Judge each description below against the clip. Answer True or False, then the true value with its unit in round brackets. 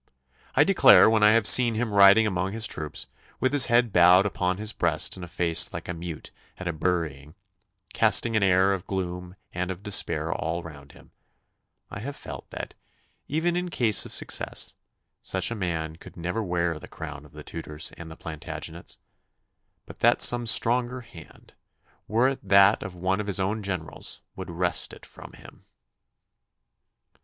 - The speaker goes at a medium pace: True (175 wpm)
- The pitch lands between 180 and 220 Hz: False (95 Hz)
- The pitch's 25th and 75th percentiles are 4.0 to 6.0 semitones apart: True (4.4 semitones)